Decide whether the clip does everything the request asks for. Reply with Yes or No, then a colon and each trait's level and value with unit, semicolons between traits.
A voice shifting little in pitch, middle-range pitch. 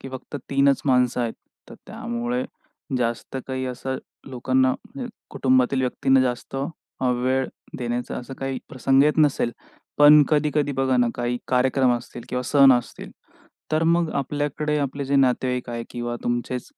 No: narrow, 2.0 semitones; low, 130 Hz